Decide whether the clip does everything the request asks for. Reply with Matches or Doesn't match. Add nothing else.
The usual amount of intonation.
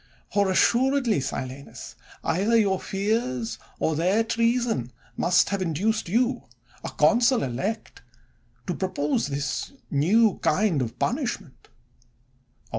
Doesn't match